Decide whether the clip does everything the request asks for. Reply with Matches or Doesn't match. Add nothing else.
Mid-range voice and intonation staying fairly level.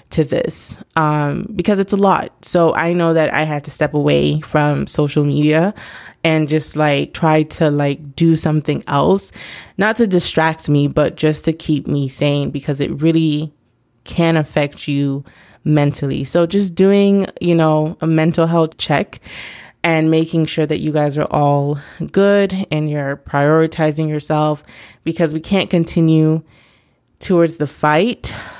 Matches